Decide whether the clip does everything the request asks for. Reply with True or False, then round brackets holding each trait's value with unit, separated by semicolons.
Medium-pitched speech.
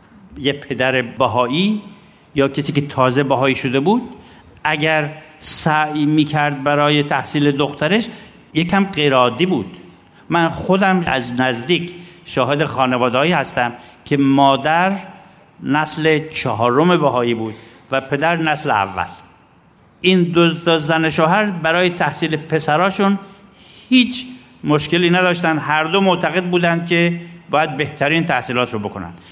True (155 Hz)